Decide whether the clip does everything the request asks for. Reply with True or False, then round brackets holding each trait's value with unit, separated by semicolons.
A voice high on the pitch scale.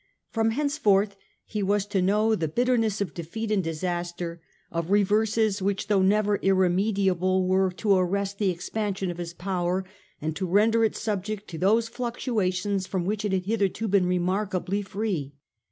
True (195 Hz)